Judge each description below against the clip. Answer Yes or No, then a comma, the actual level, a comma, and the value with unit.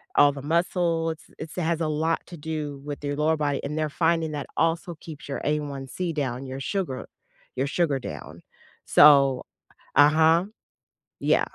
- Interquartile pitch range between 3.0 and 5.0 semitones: No, narrow, 2.5 semitones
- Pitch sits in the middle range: Yes, medium, 150 Hz